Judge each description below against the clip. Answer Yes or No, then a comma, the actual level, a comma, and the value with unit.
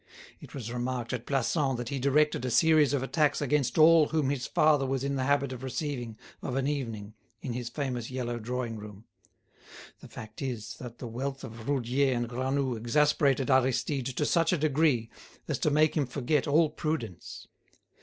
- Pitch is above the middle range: No, low, 130 Hz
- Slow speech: No, average, 185 wpm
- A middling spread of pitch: Yes, average, 3.2 semitones